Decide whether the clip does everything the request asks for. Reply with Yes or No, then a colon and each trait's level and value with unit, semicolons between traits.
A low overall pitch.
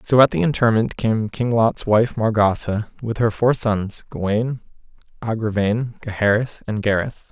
Yes: low, 110 Hz